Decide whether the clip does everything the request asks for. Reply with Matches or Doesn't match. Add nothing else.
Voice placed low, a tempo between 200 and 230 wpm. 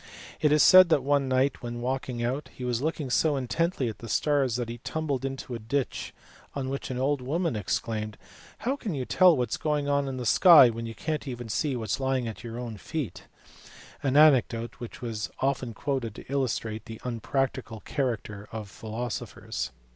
Matches